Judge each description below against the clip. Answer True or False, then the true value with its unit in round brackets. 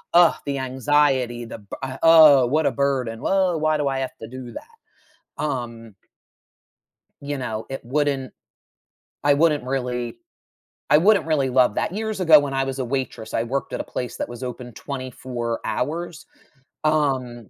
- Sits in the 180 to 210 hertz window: False (135 Hz)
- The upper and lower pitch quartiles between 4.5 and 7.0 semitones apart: False (3.6 semitones)